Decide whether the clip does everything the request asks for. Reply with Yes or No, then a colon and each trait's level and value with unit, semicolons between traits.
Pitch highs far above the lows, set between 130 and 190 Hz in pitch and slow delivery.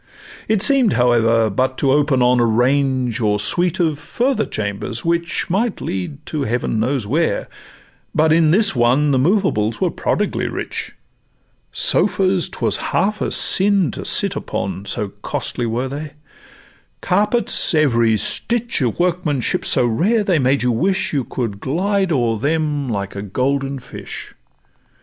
No: wide, 6.9 semitones; medium, 140 Hz; average, 150 wpm